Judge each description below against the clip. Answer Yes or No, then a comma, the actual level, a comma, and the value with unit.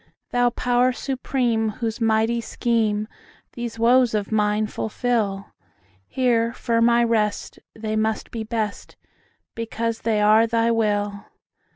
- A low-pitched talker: No, high, 225 Hz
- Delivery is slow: Yes, slow, 105 wpm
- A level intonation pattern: Yes, narrow, 1.7 semitones